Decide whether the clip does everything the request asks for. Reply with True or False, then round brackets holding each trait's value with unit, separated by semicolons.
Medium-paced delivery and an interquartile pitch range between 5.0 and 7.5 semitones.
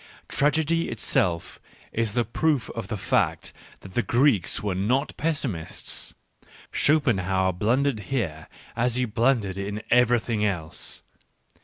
False (120 wpm; 5.4 semitones)